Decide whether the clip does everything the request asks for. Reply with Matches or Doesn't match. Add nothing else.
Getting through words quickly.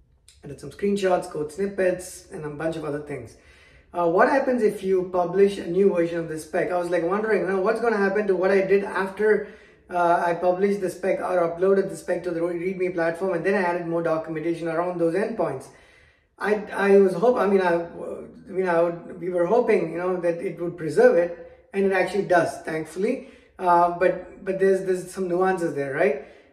Matches